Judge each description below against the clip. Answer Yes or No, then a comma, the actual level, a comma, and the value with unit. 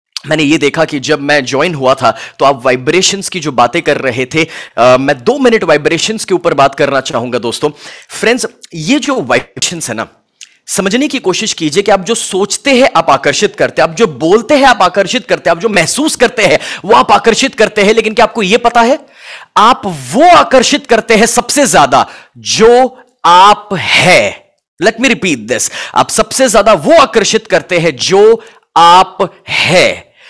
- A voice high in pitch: Yes, high, 200 Hz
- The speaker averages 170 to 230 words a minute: Yes, fast, 190 wpm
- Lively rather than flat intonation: Yes, wide, 7.9 semitones